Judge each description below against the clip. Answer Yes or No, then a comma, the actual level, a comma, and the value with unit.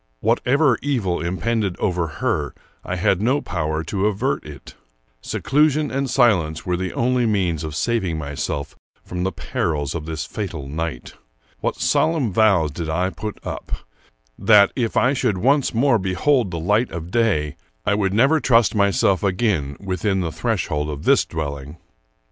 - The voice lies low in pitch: Yes, very low, 95 Hz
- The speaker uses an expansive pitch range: Yes, wide, 6.3 semitones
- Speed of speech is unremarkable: Yes, average, 160 wpm